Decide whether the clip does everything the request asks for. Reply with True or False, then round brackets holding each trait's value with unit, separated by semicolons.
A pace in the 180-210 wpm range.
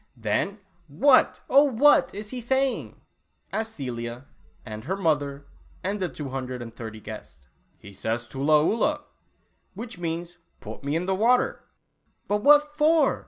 False (160 wpm)